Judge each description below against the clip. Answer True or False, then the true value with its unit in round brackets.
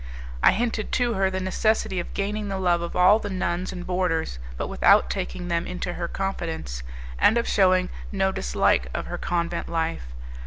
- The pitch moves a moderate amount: False (2.3 semitones)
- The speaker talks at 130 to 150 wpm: False (185 wpm)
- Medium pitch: True (180 Hz)